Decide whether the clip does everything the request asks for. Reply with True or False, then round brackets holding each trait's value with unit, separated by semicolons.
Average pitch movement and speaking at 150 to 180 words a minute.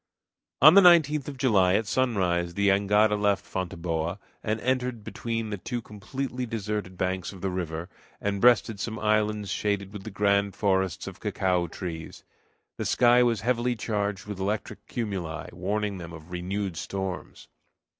True (3.4 semitones; 155 wpm)